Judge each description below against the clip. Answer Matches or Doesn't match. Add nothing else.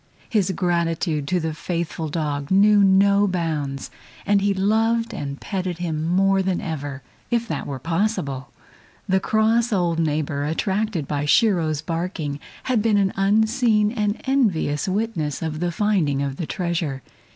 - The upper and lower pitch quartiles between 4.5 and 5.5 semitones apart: Matches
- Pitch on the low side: Doesn't match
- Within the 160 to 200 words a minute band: Doesn't match